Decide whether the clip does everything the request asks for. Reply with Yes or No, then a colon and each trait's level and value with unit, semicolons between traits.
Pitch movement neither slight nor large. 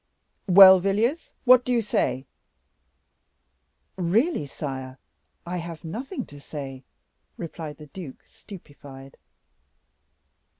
No: wide, 6.5 semitones